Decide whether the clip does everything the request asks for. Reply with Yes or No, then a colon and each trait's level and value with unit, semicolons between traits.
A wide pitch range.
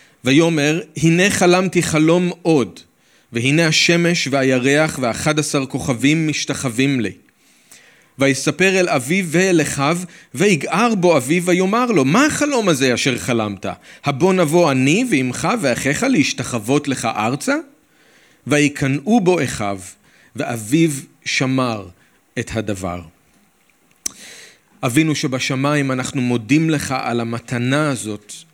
No: average, 4.7 semitones